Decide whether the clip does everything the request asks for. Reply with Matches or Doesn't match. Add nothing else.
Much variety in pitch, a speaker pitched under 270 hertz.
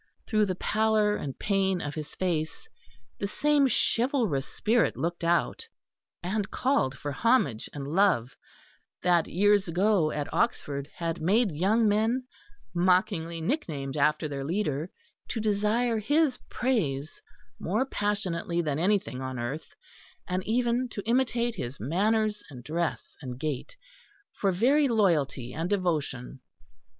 Matches